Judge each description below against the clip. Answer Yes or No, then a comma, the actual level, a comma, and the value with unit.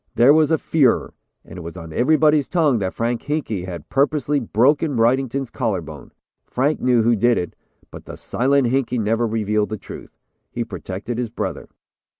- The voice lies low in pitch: Yes, low, 120 Hz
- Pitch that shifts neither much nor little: Yes, average, 4.6 semitones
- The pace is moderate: Yes, average, 175 wpm